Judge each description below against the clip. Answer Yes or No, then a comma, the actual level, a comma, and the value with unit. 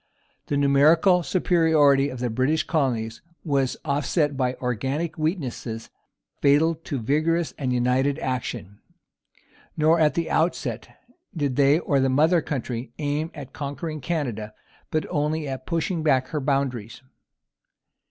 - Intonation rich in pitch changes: No, average, 3.5 semitones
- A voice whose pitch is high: No, medium, 140 Hz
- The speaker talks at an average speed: No, slow, 130 wpm